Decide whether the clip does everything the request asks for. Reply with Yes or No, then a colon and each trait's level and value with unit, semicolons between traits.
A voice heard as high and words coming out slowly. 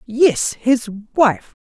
Yes: high, 240 Hz; slow, 110 wpm